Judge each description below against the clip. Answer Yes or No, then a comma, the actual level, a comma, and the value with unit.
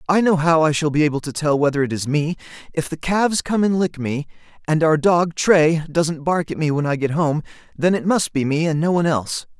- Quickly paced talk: Yes, fast, 255 wpm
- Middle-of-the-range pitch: Yes, medium, 160 Hz